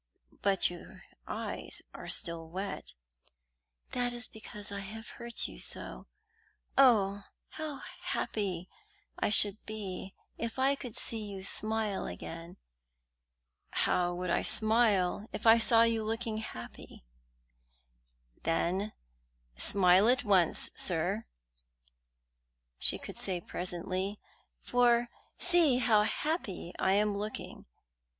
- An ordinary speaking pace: No, slow, 115 wpm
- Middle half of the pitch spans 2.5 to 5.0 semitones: Yes, average, 3.7 semitones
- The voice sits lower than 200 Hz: No, high, 210 Hz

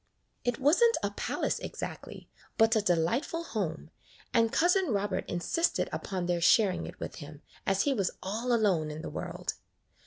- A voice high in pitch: Yes, high, 210 Hz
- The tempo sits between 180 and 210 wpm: No, average, 165 wpm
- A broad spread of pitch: Yes, wide, 6.2 semitones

